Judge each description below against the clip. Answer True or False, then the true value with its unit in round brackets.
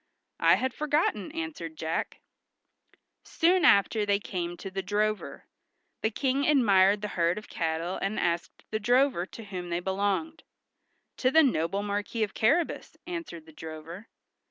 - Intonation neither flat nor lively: False (6.6 semitones)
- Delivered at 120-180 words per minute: True (150 wpm)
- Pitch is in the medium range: False (205 Hz)